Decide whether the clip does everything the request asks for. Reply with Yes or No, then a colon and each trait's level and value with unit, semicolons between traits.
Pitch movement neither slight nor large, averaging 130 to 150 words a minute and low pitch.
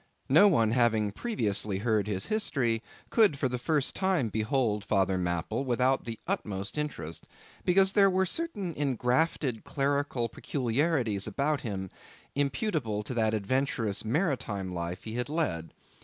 No: wide, 6.1 semitones; average, 140 wpm; low, 120 Hz